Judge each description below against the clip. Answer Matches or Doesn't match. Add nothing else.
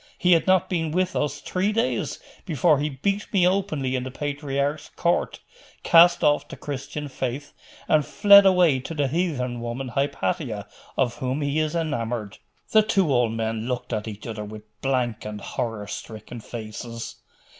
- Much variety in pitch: Matches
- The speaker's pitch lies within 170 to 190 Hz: Doesn't match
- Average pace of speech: Matches